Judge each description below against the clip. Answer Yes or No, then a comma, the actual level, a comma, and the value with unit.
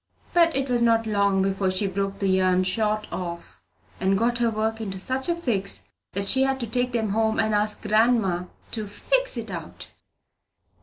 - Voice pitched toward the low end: No, high, 215 Hz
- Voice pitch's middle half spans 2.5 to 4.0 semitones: Yes, average, 3.4 semitones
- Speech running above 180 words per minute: Yes, average, 190 wpm